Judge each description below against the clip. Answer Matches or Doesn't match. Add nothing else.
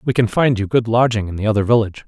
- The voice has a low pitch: Matches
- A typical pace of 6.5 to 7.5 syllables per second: Matches